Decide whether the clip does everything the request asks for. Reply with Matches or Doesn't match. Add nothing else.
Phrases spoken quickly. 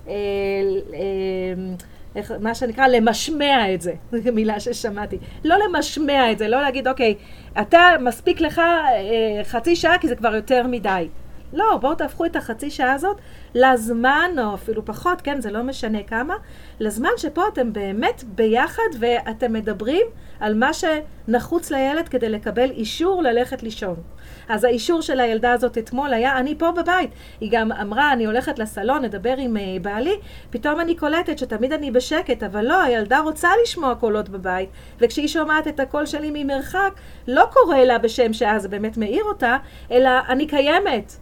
Matches